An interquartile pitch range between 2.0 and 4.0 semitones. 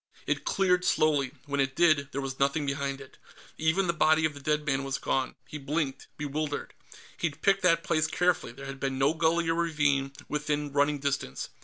Yes: narrow, 2.6 semitones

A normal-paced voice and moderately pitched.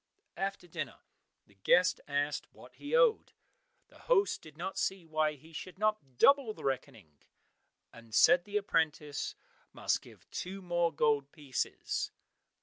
Yes: average, 145 wpm; medium, 160 Hz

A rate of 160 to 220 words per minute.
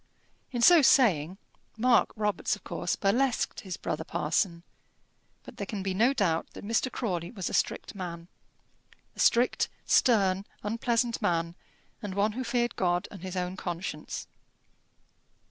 No: average, 145 wpm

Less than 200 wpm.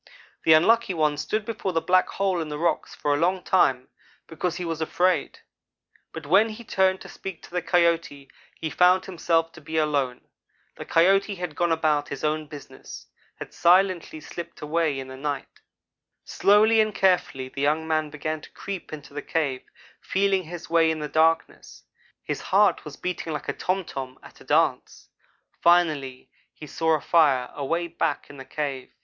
Yes: average, 180 wpm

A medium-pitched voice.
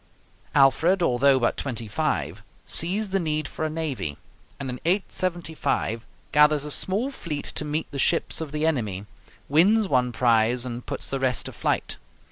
Yes: medium, 145 Hz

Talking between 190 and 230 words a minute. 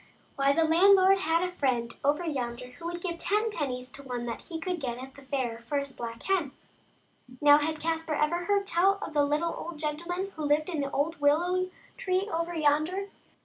Yes: fast, 205 wpm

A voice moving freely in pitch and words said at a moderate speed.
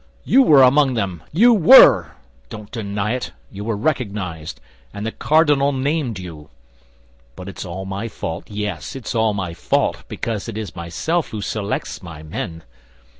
Yes: wide, 6.3 semitones; average, 155 wpm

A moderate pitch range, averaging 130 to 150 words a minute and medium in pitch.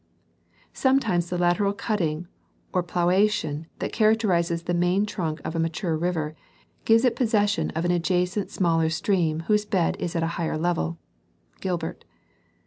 Yes: average, 3.7 semitones; average, 145 wpm; medium, 175 Hz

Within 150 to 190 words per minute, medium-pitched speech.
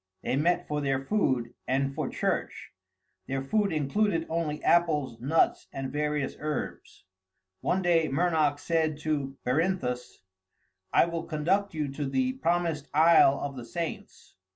No: average, 140 wpm; medium, 150 Hz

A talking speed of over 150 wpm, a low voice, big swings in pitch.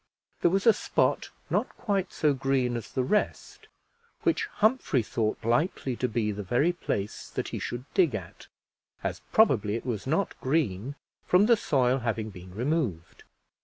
Yes: average, 165 wpm; low, 130 Hz; wide, 7.5 semitones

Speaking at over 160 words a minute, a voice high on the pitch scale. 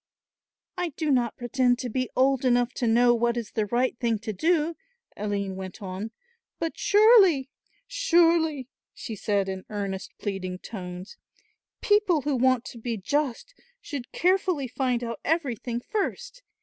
No: average, 150 wpm; high, 245 Hz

